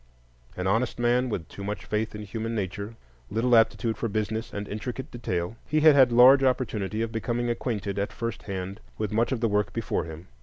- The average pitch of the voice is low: Yes, low, 110 Hz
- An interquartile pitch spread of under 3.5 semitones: Yes, average, 2.8 semitones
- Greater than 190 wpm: Yes, average, 200 wpm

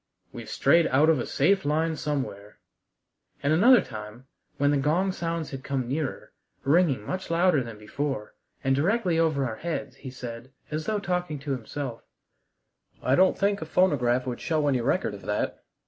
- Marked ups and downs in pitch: No, average, 4.6 semitones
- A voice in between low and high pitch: Yes, medium, 145 Hz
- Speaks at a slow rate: No, average, 175 wpm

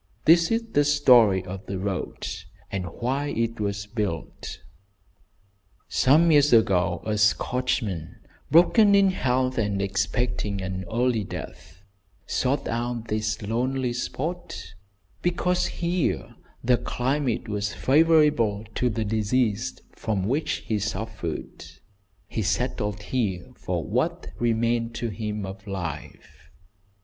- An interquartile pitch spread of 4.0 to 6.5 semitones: Yes, average, 4.4 semitones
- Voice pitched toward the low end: Yes, low, 115 Hz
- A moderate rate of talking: No, slow, 120 wpm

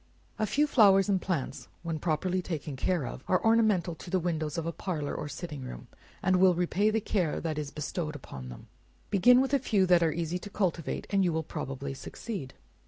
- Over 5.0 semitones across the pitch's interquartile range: No, average, 4.3 semitones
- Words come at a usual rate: No, fast, 210 wpm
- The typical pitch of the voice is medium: Yes, medium, 175 Hz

